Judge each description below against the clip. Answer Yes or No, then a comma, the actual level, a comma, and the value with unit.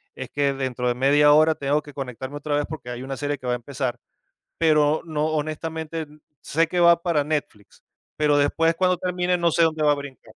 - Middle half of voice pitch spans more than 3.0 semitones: No, average, 2.7 semitones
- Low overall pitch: No, medium, 150 Hz